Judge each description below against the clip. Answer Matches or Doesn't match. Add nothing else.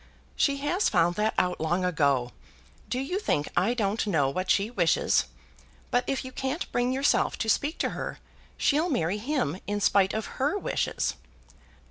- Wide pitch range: Matches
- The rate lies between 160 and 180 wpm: Matches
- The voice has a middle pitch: Doesn't match